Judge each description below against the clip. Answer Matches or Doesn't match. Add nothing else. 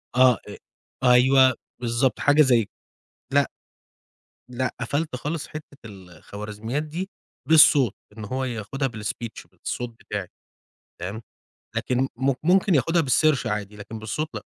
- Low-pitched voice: Matches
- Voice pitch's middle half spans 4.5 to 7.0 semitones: Matches